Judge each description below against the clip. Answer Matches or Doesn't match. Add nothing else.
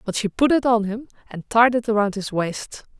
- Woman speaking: Matches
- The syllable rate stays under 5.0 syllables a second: Doesn't match